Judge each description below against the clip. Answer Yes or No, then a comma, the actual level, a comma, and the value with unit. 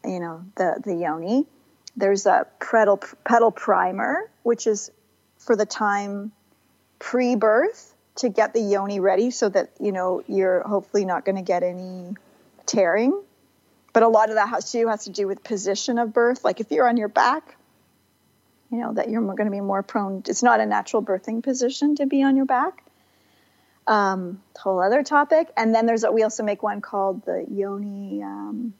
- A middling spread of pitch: Yes, average, 3.5 semitones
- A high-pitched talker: Yes, high, 215 Hz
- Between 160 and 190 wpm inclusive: Yes, average, 185 wpm